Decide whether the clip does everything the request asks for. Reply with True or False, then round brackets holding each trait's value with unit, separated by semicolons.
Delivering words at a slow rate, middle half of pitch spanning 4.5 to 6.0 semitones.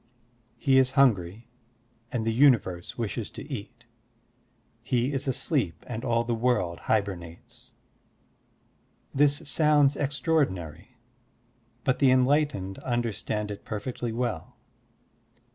True (105 wpm; 4.8 semitones)